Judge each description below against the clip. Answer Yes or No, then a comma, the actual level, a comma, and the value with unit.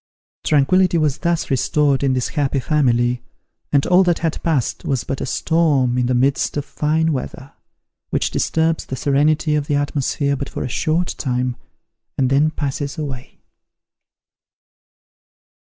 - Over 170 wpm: No, average, 150 wpm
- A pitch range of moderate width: Yes, average, 3.0 semitones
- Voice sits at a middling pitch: Yes, medium, 145 Hz